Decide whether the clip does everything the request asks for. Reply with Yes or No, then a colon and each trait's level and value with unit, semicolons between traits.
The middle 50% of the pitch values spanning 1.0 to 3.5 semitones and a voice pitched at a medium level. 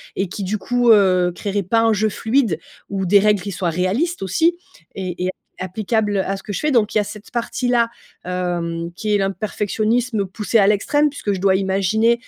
No: average, 3.1 semitones; high, 205 Hz